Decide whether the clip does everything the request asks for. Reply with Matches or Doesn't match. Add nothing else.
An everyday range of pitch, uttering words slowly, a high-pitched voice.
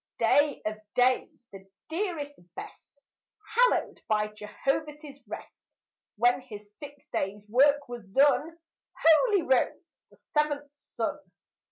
Doesn't match